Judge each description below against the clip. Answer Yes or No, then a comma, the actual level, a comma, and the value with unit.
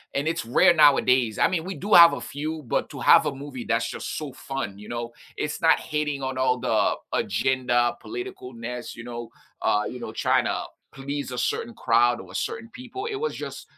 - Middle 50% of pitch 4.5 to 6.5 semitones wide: Yes, average, 5.1 semitones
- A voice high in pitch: No, low, 135 Hz